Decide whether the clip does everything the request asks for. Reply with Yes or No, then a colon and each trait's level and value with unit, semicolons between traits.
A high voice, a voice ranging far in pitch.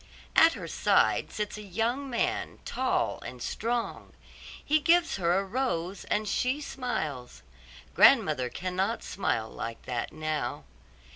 Yes: high, 210 Hz; wide, 7.8 semitones